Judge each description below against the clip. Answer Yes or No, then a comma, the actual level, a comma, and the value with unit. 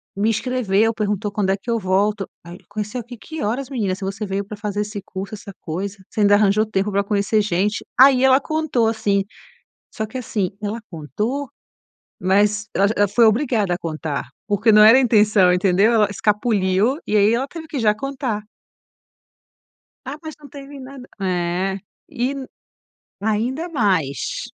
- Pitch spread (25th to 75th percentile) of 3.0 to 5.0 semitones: Yes, average, 3.5 semitones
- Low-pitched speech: No, high, 210 Hz